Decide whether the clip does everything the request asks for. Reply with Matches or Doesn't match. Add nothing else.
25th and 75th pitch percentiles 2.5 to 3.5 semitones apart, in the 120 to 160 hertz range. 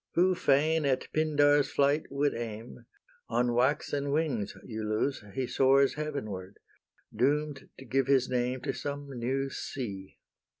Matches